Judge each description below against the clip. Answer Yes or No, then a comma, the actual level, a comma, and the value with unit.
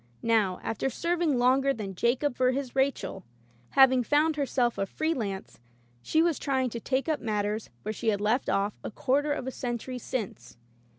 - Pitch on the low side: No, very high, 250 Hz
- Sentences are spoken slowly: No, average, 180 wpm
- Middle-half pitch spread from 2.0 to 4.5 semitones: Yes, average, 4.2 semitones